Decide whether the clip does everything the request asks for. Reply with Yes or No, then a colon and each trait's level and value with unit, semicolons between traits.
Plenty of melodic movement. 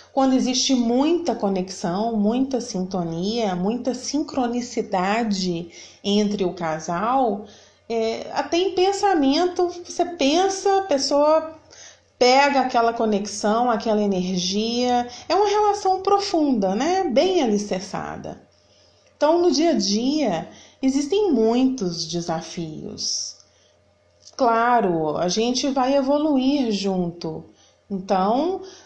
Yes: wide, 7.0 semitones